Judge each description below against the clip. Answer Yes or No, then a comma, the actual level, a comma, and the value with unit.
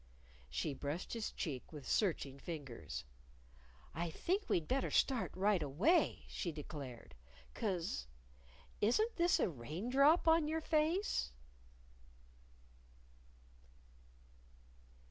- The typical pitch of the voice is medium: Yes, medium, 180 Hz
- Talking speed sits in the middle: No, slow, 100 wpm